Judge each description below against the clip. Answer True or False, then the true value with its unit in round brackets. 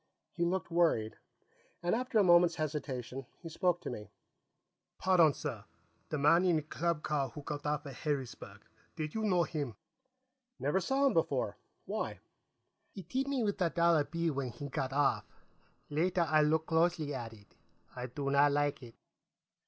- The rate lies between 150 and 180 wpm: True (170 wpm)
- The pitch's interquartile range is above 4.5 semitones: False (3.6 semitones)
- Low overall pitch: False (155 Hz)